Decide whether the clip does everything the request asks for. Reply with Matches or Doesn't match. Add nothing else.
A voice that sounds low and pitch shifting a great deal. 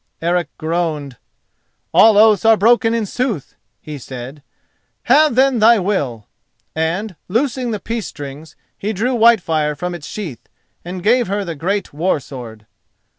Doesn't match